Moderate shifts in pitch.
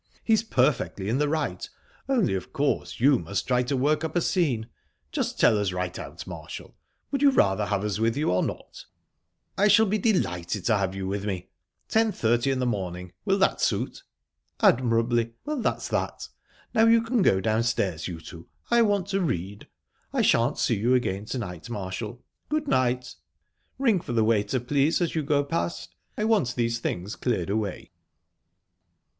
No: wide, 8.3 semitones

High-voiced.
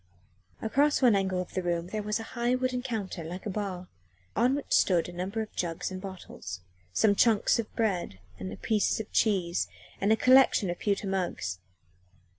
Yes: high, 200 Hz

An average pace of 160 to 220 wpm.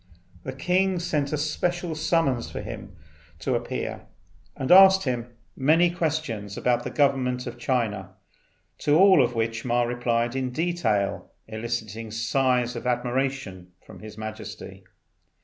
No: slow, 135 wpm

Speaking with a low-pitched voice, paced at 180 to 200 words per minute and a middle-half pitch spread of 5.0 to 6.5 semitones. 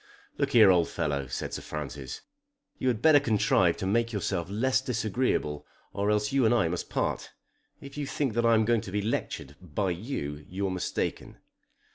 Yes: low, 105 Hz; average, 185 wpm; average, 5.3 semitones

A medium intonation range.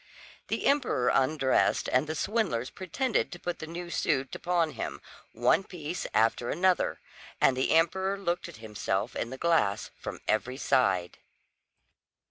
No: wide, 6.3 semitones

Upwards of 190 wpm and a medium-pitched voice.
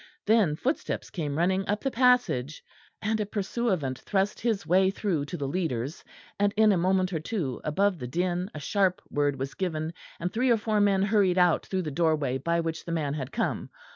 Yes: average, 200 wpm; medium, 180 Hz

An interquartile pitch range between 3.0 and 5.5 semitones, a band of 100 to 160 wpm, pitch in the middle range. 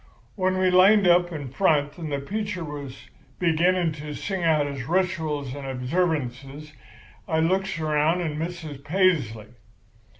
Yes: average, 4.0 semitones; average, 140 wpm; medium, 160 Hz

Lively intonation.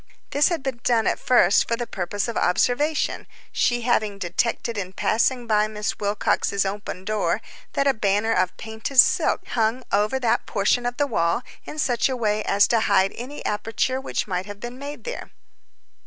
No: average, 3.5 semitones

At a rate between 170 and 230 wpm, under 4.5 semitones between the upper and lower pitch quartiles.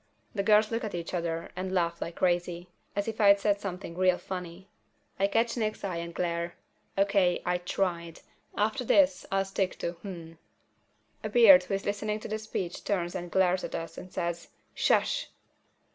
Yes: average, 180 wpm; average, 2.8 semitones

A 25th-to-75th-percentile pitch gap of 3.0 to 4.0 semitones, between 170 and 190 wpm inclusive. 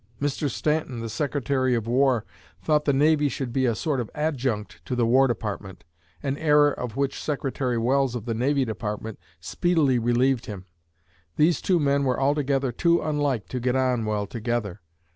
Yes: average, 3.6 semitones; average, 175 wpm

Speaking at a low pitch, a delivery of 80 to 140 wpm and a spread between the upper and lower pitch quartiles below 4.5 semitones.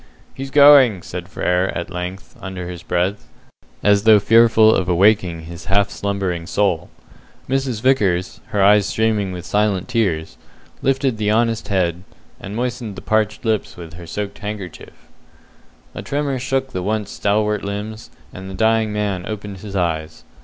No: low, 100 Hz; average, 155 wpm; average, 3.4 semitones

